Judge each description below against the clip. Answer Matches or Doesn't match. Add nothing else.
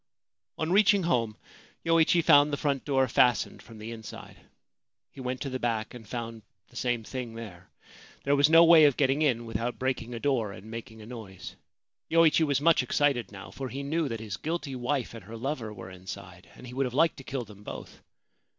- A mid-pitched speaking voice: Doesn't match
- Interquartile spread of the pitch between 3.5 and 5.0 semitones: Matches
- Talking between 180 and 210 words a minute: Matches